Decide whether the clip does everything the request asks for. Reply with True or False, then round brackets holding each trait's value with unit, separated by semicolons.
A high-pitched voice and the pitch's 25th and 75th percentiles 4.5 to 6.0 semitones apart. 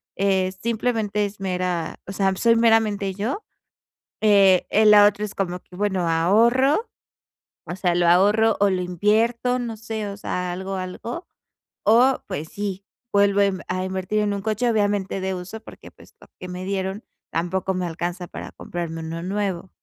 False (195 Hz; 2.8 semitones)